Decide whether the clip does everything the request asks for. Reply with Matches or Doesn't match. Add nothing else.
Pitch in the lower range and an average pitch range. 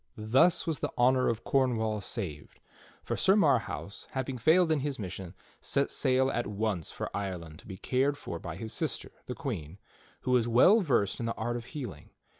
Matches